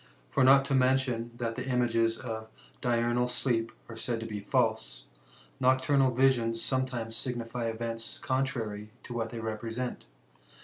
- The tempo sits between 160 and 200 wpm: No, average, 140 wpm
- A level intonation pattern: Yes, narrow, 2.3 semitones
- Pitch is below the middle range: Yes, low, 120 Hz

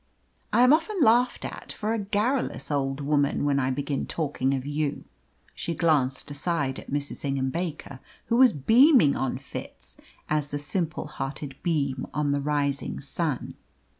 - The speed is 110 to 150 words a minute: No, average, 160 wpm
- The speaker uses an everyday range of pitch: Yes, average, 4.1 semitones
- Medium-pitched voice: Yes, medium, 145 Hz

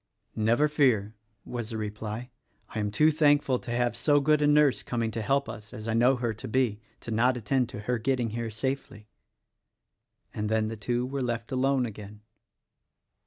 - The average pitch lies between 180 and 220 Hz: No, low, 120 Hz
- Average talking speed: Yes, average, 185 wpm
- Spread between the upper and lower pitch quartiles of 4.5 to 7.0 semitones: No, average, 3.5 semitones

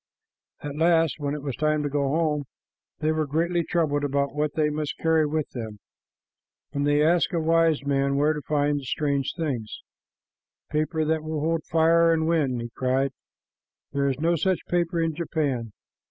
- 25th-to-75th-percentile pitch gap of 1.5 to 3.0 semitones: Yes, narrow, 2.4 semitones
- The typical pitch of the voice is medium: Yes, medium, 150 Hz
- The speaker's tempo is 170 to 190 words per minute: Yes, average, 180 wpm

